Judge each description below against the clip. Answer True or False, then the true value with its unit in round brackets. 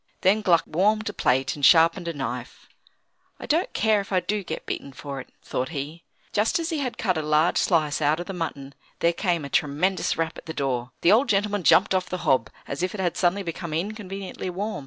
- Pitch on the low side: False (175 Hz)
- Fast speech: True (225 wpm)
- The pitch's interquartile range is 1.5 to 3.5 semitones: False (4.8 semitones)